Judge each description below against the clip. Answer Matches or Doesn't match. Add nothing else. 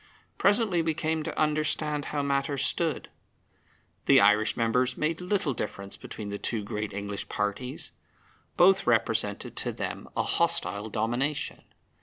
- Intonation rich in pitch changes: Matches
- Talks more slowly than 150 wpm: Matches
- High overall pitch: Doesn't match